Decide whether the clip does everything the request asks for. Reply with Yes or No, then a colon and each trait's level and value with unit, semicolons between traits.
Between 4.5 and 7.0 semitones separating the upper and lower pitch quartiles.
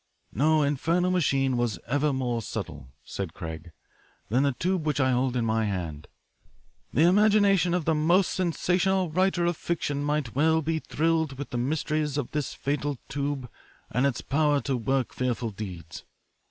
Yes: average, 4.9 semitones